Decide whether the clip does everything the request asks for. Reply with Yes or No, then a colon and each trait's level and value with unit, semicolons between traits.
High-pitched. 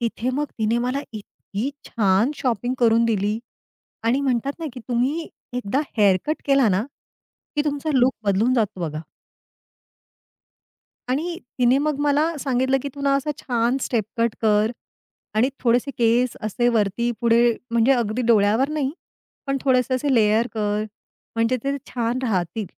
Yes: high, 240 Hz